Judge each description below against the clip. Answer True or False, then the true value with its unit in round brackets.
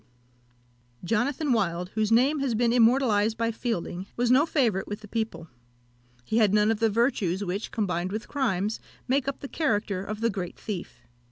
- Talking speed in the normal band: True (175 wpm)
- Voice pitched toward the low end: False (220 Hz)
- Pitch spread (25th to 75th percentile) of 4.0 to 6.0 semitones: False (3.4 semitones)